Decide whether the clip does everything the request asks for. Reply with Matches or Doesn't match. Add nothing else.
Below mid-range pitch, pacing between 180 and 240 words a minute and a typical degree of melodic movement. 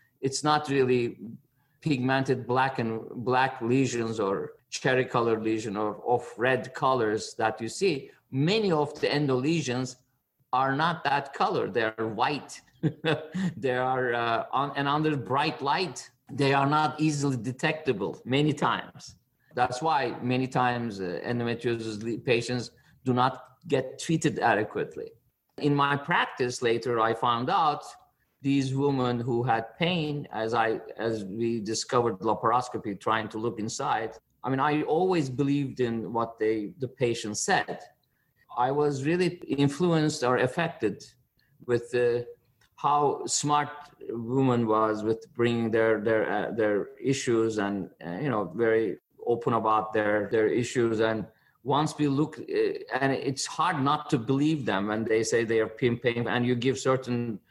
Doesn't match